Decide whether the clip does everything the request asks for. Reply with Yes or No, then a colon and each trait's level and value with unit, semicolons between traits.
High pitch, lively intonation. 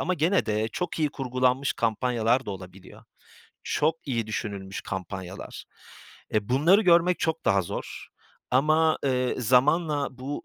No: low, 130 Hz; wide, 6.5 semitones